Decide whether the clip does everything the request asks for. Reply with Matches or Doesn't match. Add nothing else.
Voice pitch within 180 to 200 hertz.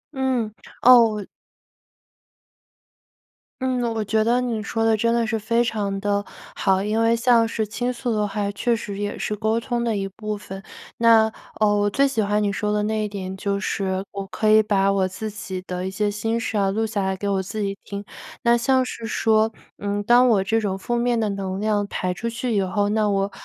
Doesn't match